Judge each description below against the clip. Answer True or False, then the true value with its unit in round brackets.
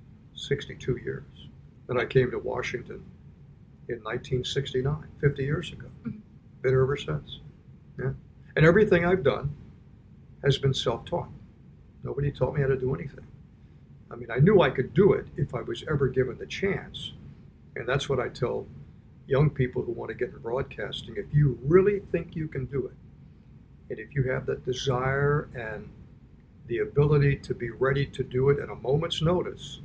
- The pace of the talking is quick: False (170 wpm)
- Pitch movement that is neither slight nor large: False (2.3 semitones)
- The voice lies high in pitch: False (135 Hz)